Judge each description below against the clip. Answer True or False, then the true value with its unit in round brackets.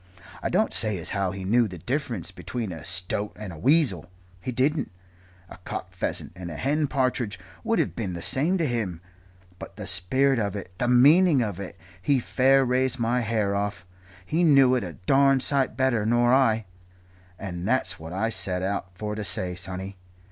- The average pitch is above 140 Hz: False (110 Hz)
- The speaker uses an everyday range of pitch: False (5.9 semitones)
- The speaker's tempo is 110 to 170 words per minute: False (190 wpm)